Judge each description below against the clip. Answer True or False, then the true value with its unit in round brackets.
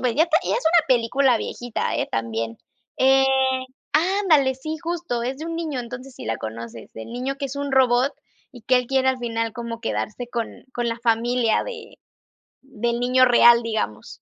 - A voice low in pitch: False (250 Hz)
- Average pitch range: True (3.1 semitones)